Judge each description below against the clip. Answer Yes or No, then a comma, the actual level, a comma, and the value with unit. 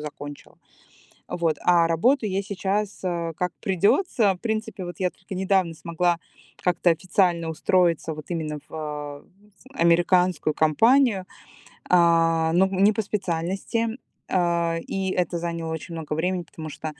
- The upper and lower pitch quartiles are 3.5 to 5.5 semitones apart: No, average, 2.7 semitones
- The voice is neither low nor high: Yes, medium, 175 Hz